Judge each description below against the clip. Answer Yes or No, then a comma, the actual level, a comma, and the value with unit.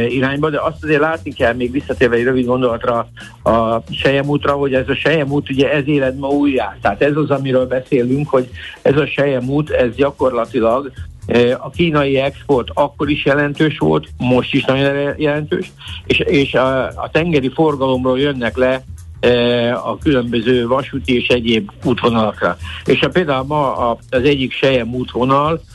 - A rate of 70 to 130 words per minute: No, fast, 155 wpm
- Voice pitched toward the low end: Yes, low, 130 Hz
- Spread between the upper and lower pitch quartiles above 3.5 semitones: No, average, 2.9 semitones